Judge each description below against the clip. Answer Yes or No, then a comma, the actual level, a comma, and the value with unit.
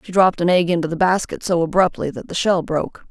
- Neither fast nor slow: No, fast, 250 wpm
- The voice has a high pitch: No, medium, 175 Hz